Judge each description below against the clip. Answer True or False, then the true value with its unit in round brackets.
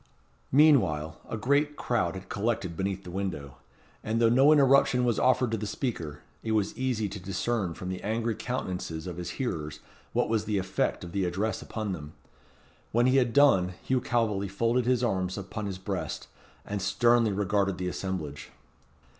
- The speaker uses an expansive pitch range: False (4.6 semitones)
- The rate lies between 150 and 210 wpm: True (175 wpm)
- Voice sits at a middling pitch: False (105 Hz)